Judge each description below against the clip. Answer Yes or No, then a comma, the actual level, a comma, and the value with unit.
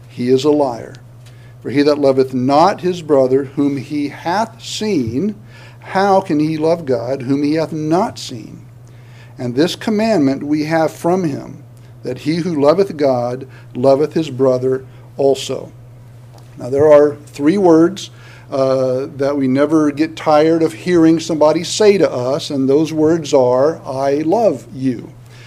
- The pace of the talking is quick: No, average, 155 wpm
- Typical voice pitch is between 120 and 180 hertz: Yes, medium, 140 Hz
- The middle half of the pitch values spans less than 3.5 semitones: No, average, 4.0 semitones